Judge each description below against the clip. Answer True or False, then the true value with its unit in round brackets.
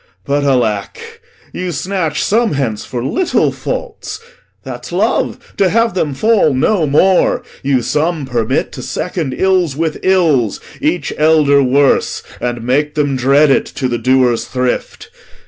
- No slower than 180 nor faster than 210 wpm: False (145 wpm)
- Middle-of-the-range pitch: True (145 Hz)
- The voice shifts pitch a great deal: True (5.8 semitones)